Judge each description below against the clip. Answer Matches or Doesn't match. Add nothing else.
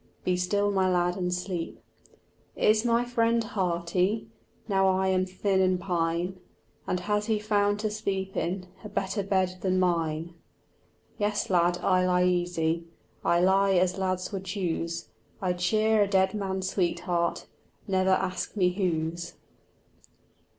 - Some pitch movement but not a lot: Doesn't match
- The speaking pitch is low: Doesn't match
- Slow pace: Doesn't match